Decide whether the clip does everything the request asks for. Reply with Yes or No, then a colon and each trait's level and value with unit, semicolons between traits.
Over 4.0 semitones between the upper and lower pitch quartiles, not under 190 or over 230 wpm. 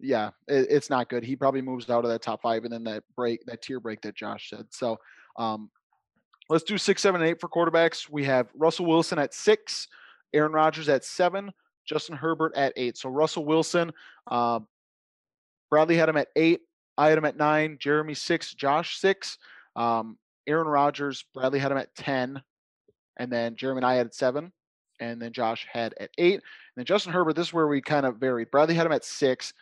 Yes: average, 5.1 semitones; fast, 205 wpm